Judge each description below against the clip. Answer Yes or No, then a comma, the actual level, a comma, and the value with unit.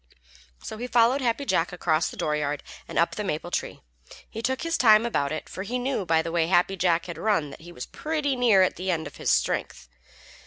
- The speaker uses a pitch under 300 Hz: Yes, high, 190 Hz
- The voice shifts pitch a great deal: Yes, wide, 6.9 semitones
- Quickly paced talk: Yes, fast, 230 wpm